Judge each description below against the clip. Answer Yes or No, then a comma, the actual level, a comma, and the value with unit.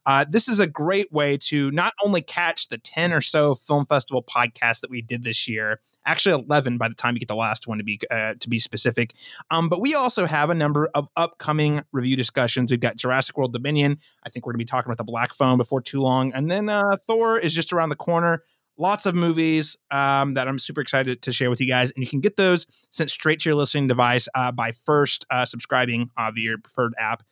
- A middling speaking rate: No, fast, 245 wpm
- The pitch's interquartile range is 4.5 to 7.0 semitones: Yes, average, 4.8 semitones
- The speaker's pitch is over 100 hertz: Yes, medium, 140 Hz